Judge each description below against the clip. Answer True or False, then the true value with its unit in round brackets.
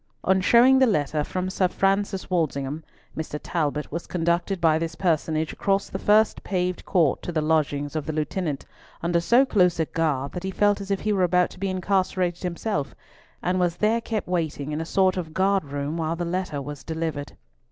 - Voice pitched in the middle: True (175 Hz)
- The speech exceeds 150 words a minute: True (200 wpm)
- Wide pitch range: False (3.4 semitones)